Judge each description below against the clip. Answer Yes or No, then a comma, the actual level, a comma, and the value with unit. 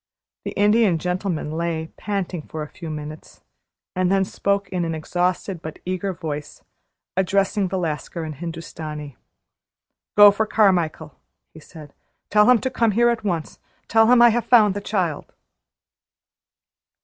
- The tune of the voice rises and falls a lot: No, average, 4.4 semitones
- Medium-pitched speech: Yes, medium, 180 Hz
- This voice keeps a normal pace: Yes, average, 150 wpm